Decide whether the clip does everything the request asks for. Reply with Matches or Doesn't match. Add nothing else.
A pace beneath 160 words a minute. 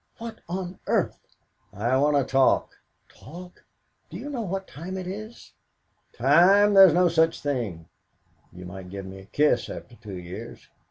Doesn't match